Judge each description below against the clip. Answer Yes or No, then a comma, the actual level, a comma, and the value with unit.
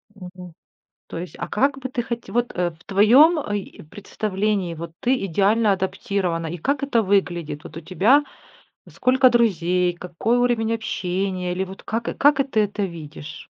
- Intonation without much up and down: No, average, 4.9 semitones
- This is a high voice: Yes, high, 200 Hz